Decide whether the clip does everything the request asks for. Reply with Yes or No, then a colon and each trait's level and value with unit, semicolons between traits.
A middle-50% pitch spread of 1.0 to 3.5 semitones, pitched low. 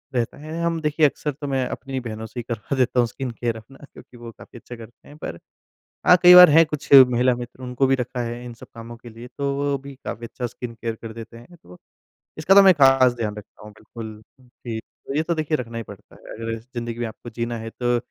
Yes: average, 3.2 semitones; low, 120 Hz